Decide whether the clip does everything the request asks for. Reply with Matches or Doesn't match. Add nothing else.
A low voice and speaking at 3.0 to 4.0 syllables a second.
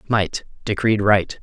Matches